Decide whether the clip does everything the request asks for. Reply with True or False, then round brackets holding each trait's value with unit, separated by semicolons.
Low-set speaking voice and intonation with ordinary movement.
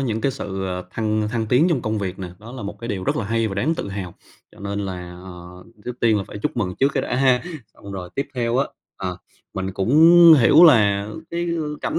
True (105 Hz; 4.5 semitones)